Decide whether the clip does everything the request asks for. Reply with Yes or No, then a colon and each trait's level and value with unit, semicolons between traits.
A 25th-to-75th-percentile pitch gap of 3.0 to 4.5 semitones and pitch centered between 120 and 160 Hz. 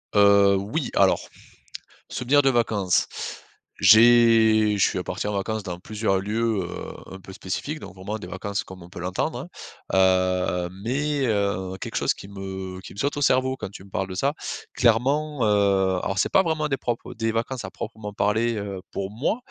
No: average, 3.7 semitones; low, 105 Hz